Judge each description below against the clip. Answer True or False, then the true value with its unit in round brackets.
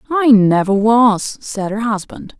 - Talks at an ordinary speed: True (150 wpm)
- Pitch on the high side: True (220 Hz)